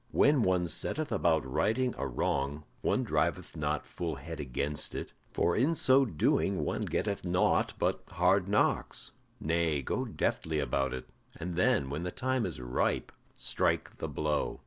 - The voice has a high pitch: No, very low, 85 Hz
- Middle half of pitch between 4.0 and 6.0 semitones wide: Yes, average, 4.9 semitones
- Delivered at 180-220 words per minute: No, average, 160 wpm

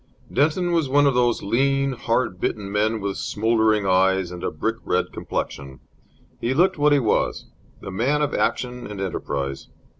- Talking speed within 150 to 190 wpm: Yes, average, 170 wpm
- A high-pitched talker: No, low, 115 Hz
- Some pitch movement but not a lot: No, wide, 6.0 semitones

